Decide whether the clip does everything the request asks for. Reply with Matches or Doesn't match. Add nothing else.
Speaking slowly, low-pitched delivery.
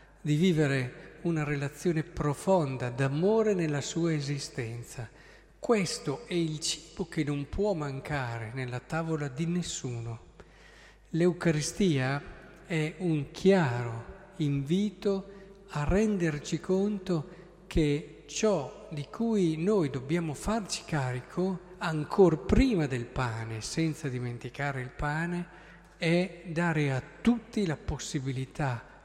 Doesn't match